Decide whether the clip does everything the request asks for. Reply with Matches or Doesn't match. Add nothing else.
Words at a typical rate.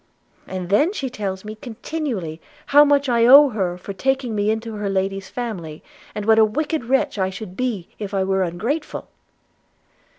Matches